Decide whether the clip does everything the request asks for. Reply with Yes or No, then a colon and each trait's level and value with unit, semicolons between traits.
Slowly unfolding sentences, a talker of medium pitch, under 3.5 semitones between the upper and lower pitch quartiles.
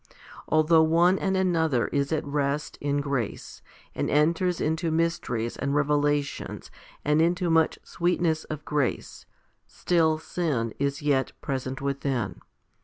Yes: slow, 130 wpm; medium, 150 Hz; average, 2.8 semitones